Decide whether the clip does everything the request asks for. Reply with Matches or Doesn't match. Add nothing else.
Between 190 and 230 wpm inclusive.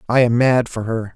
Doesn't match